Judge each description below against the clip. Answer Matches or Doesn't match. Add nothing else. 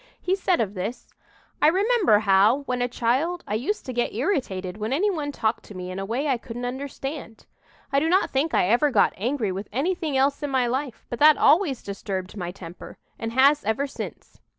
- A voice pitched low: Doesn't match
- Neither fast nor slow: Doesn't match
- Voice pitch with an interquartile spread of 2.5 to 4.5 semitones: Doesn't match